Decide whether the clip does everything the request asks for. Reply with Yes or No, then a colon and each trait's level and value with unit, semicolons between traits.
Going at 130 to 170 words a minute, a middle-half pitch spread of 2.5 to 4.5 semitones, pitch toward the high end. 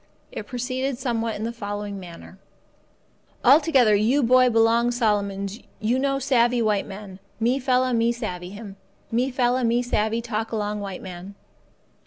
Yes: average, 150 wpm; average, 3.3 semitones; high, 230 Hz